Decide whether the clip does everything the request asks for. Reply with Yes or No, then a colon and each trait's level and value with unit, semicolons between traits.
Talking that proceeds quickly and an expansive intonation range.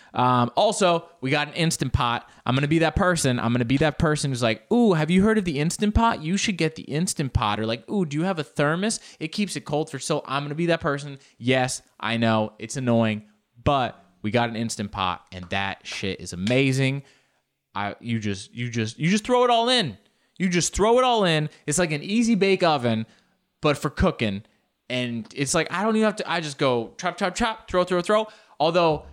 Yes: fast, 230 wpm; wide, 7.2 semitones